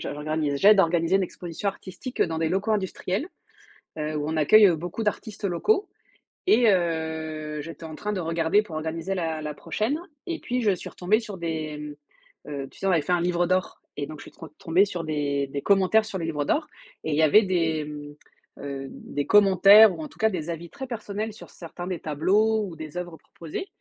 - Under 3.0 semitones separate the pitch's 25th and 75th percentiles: No, average, 4.5 semitones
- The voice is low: No, medium, 170 Hz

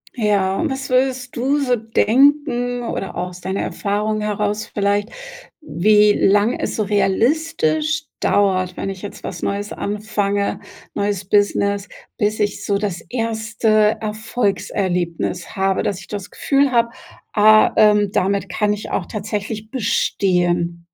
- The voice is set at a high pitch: Yes, high, 210 Hz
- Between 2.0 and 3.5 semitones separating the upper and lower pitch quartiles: Yes, narrow, 2.6 semitones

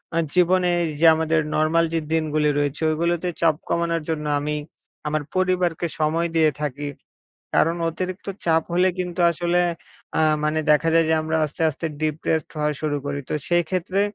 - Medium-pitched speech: Yes, medium, 160 Hz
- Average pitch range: No, narrow, 2.1 semitones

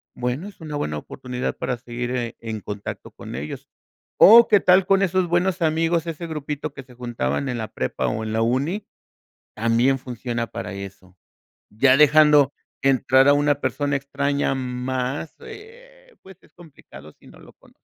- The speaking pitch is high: No, low, 135 Hz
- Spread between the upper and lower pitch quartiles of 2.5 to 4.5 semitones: No, average, 5.3 semitones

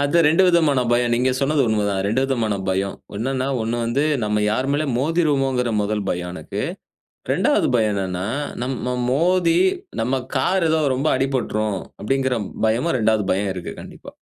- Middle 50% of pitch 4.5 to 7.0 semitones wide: Yes, average, 4.9 semitones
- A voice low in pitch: Yes, low, 125 Hz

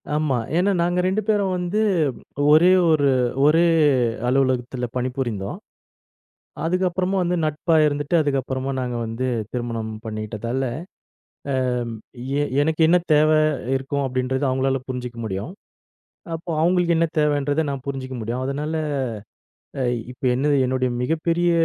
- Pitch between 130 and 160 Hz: Yes, medium, 140 Hz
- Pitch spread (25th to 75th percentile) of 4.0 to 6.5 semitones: Yes, average, 4.5 semitones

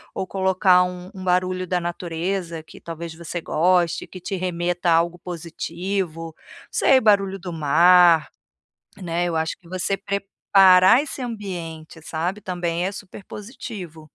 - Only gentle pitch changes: Yes, narrow, 2.2 semitones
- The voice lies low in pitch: No, medium, 180 Hz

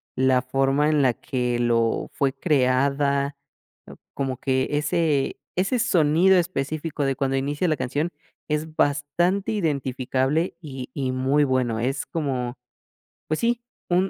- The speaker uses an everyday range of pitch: Yes, average, 3.2 semitones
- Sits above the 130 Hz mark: Yes, medium, 140 Hz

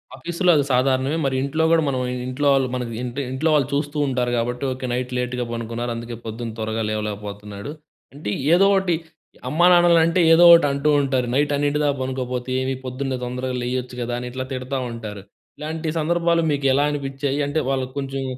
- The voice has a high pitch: No, low, 130 Hz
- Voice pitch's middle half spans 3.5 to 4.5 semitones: No, average, 2.9 semitones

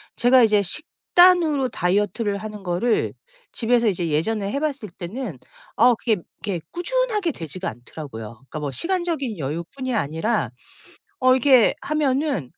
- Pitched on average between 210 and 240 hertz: Yes, high, 225 Hz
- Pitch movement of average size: No, wide, 8.0 semitones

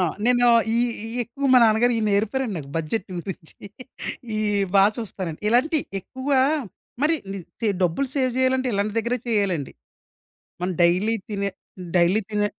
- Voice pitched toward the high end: Yes, high, 220 Hz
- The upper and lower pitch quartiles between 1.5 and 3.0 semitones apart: No, average, 4.2 semitones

